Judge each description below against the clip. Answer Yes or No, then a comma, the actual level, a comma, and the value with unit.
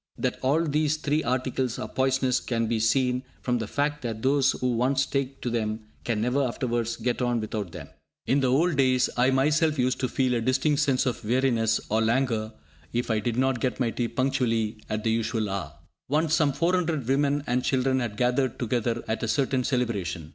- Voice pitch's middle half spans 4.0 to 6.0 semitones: No, average, 2.8 semitones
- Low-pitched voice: Yes, low, 125 Hz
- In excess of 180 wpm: Yes, average, 200 wpm